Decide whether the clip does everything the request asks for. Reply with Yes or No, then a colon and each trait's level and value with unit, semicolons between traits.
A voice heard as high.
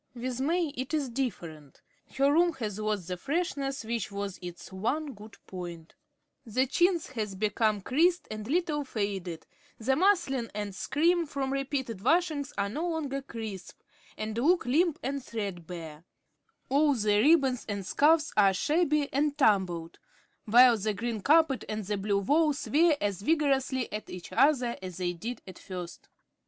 Yes: high, 245 Hz